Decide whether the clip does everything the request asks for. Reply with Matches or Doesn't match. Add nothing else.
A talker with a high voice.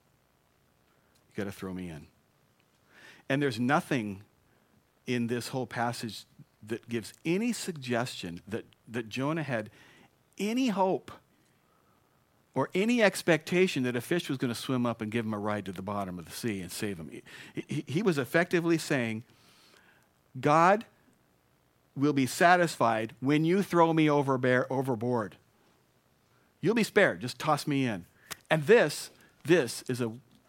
Doesn't match